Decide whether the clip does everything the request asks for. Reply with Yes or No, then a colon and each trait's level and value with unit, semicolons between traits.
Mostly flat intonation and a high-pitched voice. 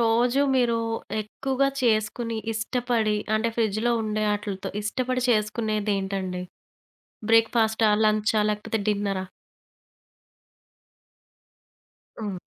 Yes: narrow, 1.9 semitones; high, 220 Hz